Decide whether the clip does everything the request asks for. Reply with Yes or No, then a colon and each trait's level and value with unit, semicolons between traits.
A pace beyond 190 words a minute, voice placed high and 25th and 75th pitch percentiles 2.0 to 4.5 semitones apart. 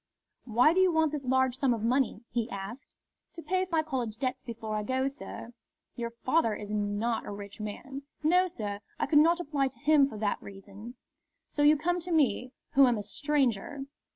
No: average, 200 wpm; very high, 260 Hz; wide, 5.5 semitones